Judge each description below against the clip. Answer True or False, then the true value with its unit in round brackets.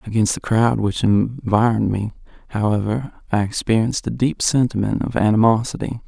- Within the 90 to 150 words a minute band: True (140 wpm)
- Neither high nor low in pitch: False (110 Hz)